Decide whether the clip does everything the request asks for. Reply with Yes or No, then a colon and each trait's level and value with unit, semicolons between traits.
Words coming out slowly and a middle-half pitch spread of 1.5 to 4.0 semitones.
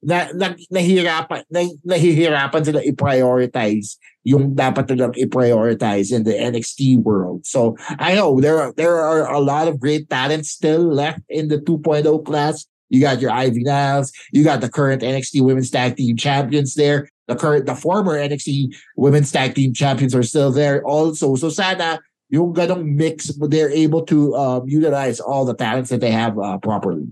No: average, 175 wpm; average, 3.3 semitones